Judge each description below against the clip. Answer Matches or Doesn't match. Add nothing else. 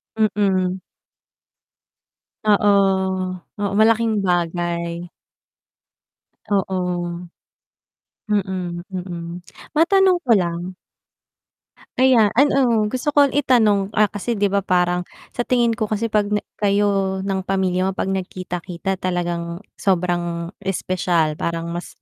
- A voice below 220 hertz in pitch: Matches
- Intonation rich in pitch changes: Doesn't match